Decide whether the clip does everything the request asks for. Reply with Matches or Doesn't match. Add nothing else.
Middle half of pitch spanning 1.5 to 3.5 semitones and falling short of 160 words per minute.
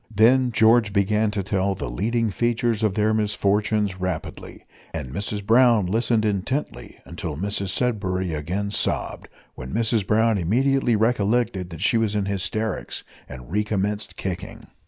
Matches